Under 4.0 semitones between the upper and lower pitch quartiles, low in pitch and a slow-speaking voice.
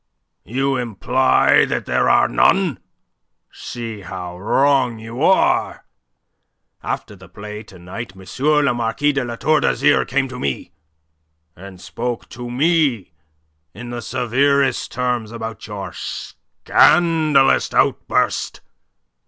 No: average, 4.3 semitones; low, 120 Hz; slow, 120 wpm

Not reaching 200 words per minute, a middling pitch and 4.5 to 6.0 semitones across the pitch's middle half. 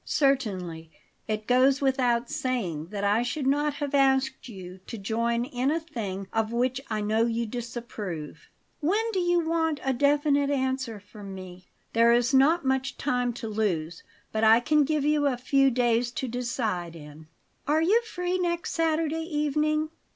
No: average, 165 wpm; very high, 250 Hz; average, 5.1 semitones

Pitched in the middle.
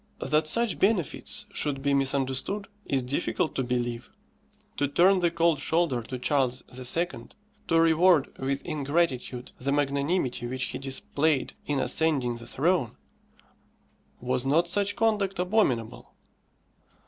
Yes: medium, 145 Hz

